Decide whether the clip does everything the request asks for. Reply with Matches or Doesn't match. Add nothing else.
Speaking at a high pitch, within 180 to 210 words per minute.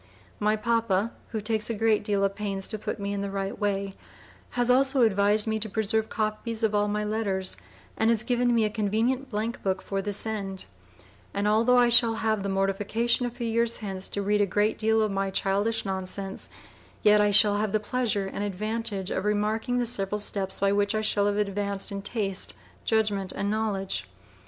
Matches